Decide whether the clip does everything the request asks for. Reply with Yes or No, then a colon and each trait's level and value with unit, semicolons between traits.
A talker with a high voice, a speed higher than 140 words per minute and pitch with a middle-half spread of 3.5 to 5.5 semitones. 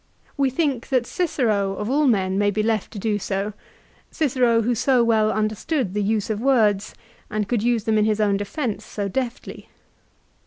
No: high, 220 Hz; average, 185 wpm; average, 3.1 semitones